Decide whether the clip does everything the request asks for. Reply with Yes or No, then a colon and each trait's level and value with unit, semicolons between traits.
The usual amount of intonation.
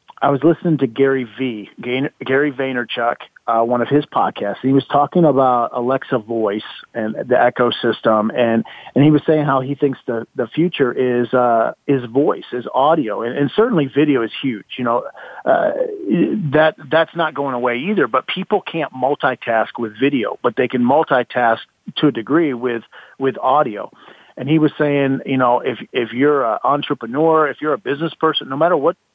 Yes: average, 3.6 semitones